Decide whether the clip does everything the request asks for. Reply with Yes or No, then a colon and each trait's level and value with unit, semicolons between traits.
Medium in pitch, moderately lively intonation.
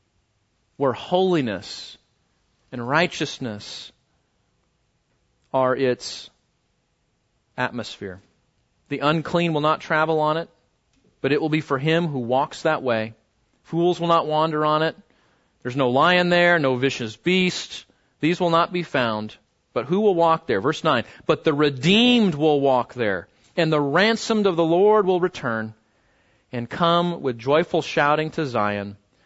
No: medium, 150 Hz; wide, 5.7 semitones